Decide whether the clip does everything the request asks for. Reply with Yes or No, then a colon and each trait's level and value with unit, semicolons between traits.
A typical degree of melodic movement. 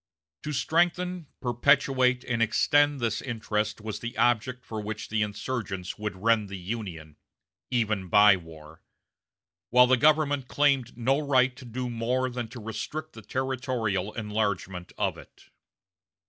Yes: average, 3.6 semitones